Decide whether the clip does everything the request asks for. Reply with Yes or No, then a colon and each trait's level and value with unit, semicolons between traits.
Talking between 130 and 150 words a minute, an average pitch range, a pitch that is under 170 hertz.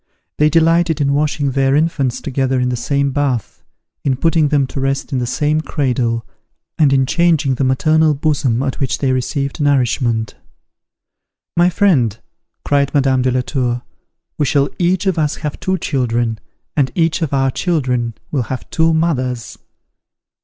No: average, 160 wpm; average, 3.4 semitones; medium, 140 Hz